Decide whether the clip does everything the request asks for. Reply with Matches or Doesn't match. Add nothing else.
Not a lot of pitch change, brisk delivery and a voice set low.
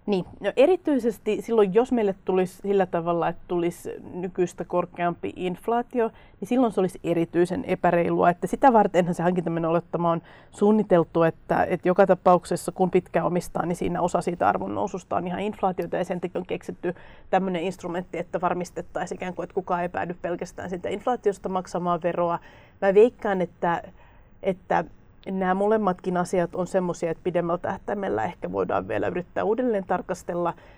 Doesn't match